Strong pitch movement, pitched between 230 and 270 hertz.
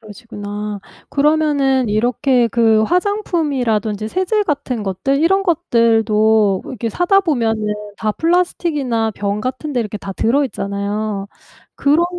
Yes: wide, 5.9 semitones; high, 235 Hz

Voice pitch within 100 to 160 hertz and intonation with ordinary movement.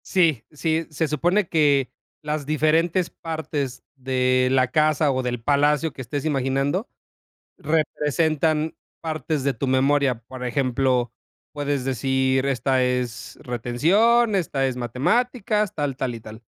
Yes: medium, 140 Hz; average, 3.6 semitones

